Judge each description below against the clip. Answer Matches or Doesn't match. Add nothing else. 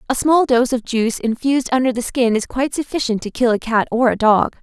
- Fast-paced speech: Matches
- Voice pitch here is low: Doesn't match